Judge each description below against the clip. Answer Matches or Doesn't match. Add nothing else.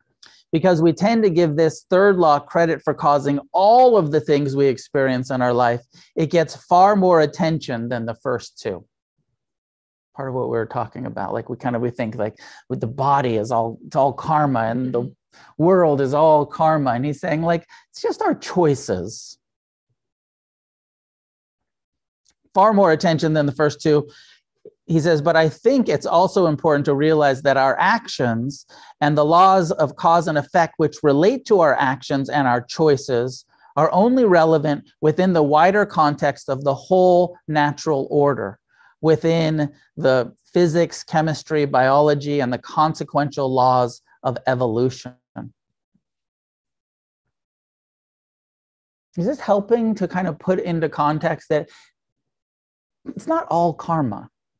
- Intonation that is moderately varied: Matches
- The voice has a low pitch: Doesn't match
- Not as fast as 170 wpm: Matches